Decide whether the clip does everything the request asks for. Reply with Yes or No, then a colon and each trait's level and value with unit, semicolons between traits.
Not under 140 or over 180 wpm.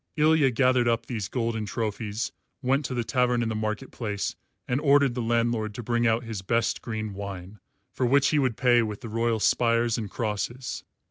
No: average, 195 wpm